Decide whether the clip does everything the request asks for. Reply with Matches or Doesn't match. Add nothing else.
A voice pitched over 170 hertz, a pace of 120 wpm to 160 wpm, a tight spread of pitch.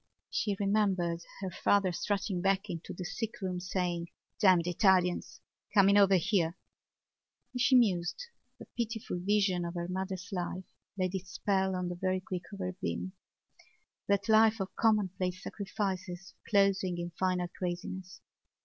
Matches